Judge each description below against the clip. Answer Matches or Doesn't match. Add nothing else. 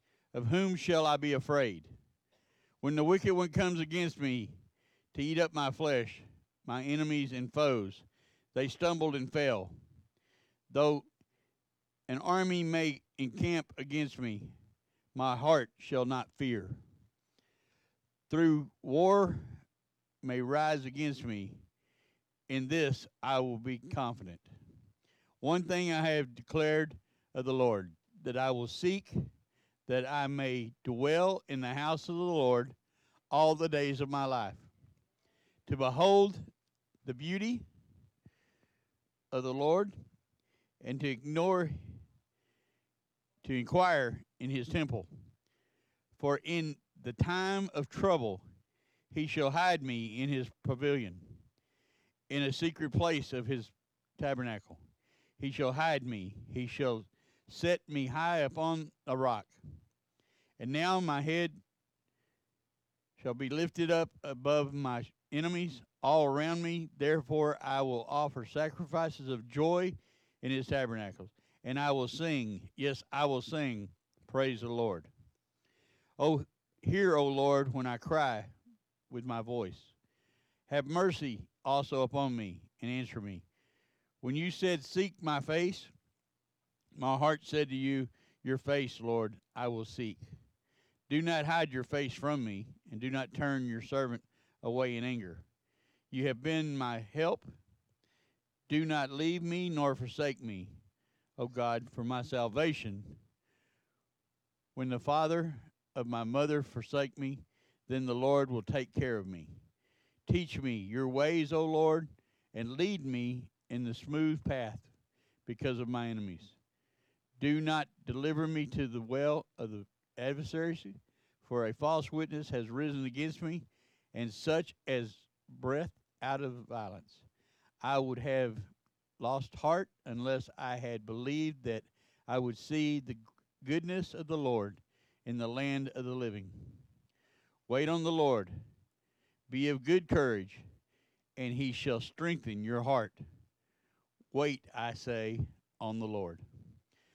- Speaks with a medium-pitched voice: Doesn't match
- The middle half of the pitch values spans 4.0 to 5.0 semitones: Matches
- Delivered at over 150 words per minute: Doesn't match